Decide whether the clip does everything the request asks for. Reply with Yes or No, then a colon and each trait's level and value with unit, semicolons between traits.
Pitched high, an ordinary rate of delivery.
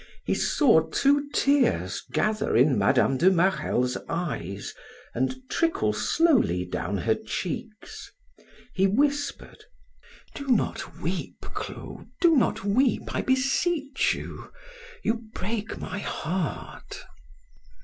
No: high, 205 Hz; slow, 110 wpm